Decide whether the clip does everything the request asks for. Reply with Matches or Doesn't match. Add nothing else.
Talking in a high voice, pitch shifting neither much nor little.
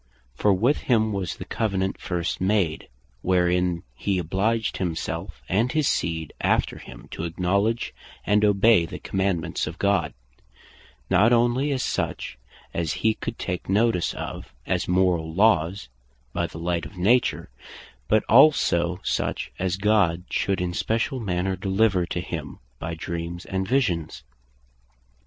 Doesn't match